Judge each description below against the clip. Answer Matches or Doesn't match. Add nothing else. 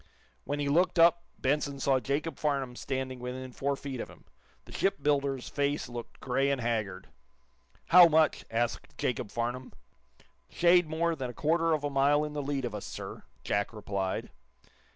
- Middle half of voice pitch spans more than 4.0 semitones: Doesn't match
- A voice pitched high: Doesn't match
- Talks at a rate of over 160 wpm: Matches